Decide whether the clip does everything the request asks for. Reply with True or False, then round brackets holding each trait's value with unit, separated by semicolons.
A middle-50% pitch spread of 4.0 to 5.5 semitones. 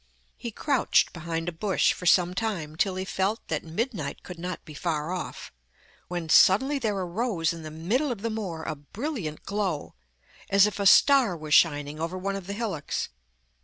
True (4.5 semitones)